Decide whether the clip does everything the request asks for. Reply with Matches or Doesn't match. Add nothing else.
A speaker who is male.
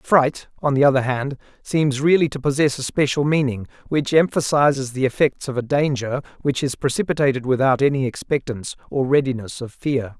Matches